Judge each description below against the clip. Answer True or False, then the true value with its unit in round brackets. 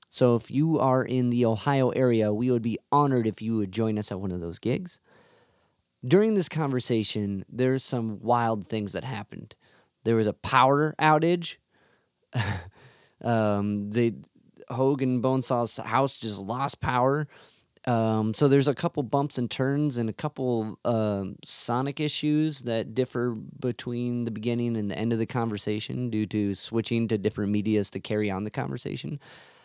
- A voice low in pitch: True (120 Hz)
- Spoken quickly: False (160 wpm)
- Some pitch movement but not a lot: True (3.4 semitones)